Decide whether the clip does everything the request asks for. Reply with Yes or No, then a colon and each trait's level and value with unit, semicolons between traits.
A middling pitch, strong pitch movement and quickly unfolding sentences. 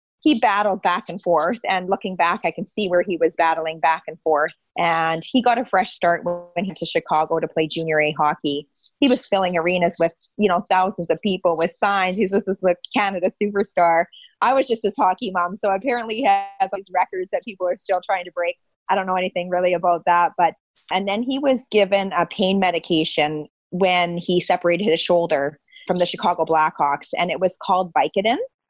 No: medium, 180 Hz; average, 3.0 semitones; fast, 210 wpm